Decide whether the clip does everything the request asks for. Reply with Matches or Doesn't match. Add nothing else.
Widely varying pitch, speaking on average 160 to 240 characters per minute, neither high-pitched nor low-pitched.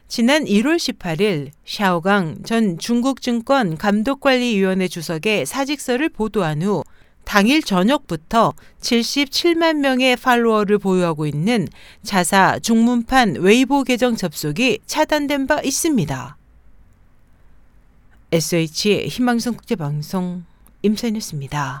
Doesn't match